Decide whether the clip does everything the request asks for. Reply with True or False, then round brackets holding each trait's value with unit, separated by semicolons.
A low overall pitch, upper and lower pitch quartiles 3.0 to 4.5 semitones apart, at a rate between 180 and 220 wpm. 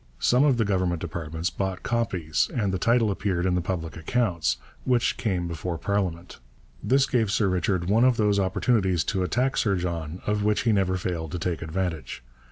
True (95 Hz; 3.7 semitones; 185 wpm)